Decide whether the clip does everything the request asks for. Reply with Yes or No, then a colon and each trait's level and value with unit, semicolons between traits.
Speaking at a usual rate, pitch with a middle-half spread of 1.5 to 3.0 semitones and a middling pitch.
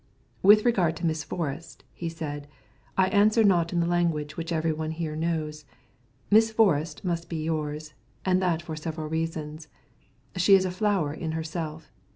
Yes: average, 170 wpm; narrow, 2.5 semitones; medium, 165 Hz